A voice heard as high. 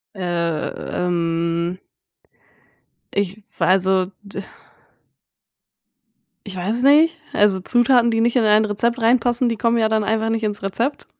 Yes: high, 215 Hz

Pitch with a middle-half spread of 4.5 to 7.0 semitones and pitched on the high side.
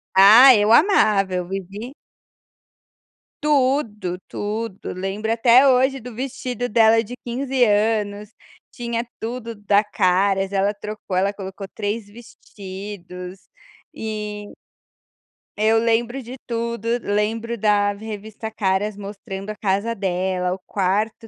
No: average, 2.8 semitones; high, 210 Hz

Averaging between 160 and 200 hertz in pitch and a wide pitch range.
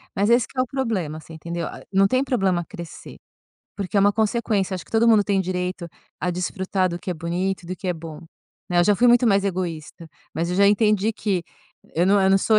No: high, 190 Hz; average, 3.2 semitones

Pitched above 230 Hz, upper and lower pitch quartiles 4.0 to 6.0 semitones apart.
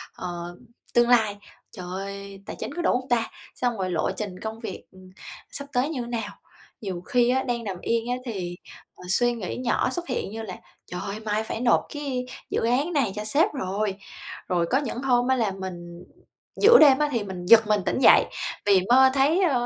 No: high, 225 Hz; average, 4.7 semitones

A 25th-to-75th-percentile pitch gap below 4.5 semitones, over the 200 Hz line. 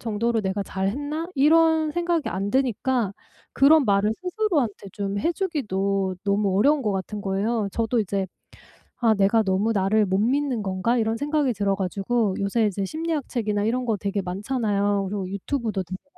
No: average, 5.3 semitones; high, 215 Hz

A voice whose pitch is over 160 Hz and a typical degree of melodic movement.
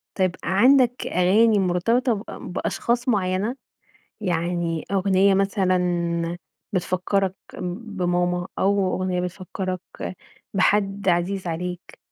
No: high, 190 Hz; narrow, 2.1 semitones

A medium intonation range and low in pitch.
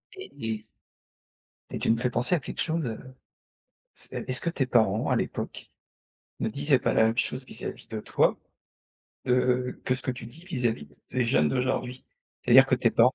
No: narrow, 2.3 semitones; low, 125 Hz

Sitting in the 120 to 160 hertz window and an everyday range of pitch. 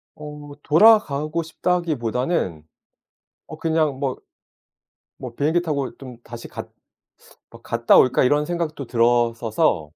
Yes: medium, 140 Hz; average, 5.0 semitones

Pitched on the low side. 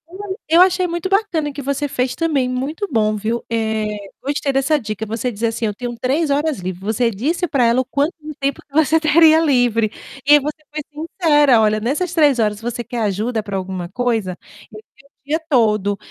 No: very high, 255 Hz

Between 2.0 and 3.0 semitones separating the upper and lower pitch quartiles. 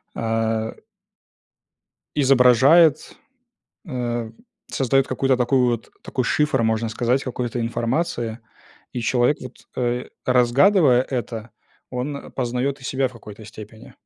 Yes: narrow, 2.5 semitones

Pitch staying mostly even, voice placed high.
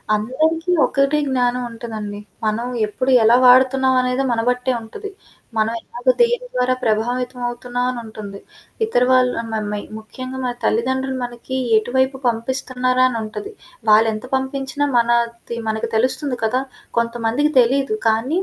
Yes: narrow, 2.3 semitones; very high, 250 Hz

